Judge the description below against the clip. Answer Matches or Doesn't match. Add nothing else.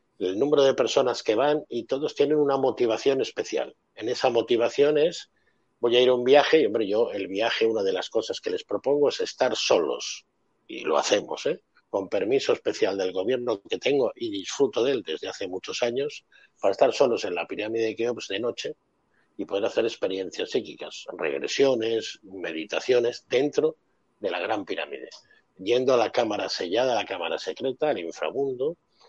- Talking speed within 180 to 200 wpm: Matches